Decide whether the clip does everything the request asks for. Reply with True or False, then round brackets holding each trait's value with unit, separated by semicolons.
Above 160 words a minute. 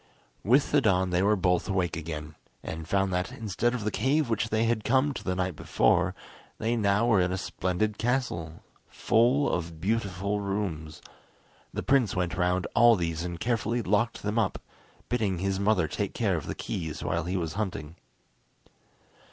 True (175 wpm)